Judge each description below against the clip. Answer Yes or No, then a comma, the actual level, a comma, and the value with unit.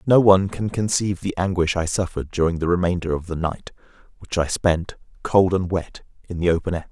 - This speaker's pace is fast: Yes, fast, 210 wpm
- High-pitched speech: No, very low, 90 Hz